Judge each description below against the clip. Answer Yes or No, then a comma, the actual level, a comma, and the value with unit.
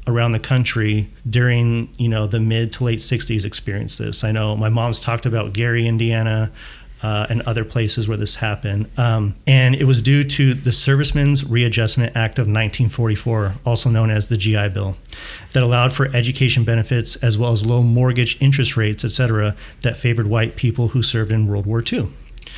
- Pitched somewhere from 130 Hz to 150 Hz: No, low, 115 Hz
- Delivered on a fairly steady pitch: Yes, narrow, 2.1 semitones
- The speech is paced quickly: No, average, 185 wpm